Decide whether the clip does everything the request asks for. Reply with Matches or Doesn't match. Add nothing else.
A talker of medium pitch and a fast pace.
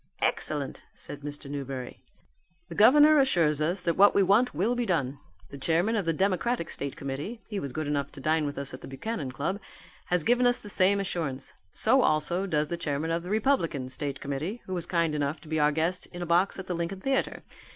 Matches